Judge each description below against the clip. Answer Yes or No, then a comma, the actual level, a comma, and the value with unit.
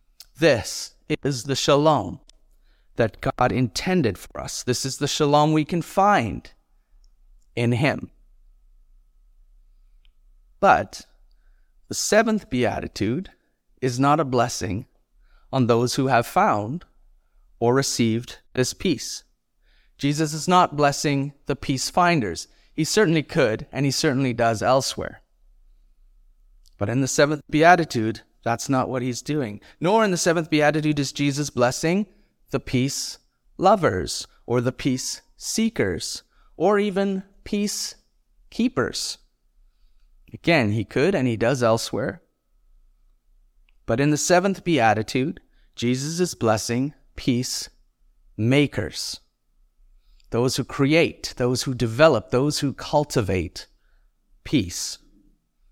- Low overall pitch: Yes, low, 130 Hz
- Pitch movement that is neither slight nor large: No, wide, 8.2 semitones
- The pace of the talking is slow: Yes, slow, 115 wpm